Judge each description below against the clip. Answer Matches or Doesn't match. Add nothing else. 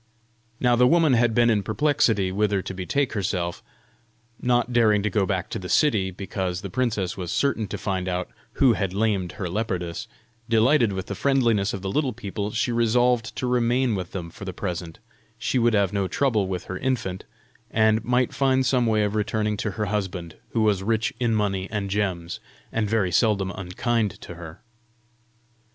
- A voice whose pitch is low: Matches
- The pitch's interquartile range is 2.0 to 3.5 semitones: Doesn't match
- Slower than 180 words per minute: Doesn't match